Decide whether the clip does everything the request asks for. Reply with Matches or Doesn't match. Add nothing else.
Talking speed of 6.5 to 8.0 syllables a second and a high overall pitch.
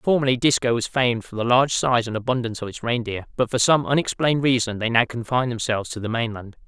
Doesn't match